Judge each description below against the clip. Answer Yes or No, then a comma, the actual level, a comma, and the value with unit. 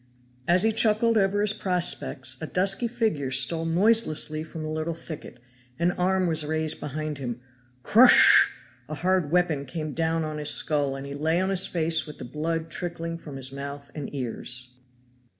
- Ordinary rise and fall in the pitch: Yes, average, 3.8 semitones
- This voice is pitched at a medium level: Yes, medium, 160 Hz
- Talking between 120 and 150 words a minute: No, average, 175 wpm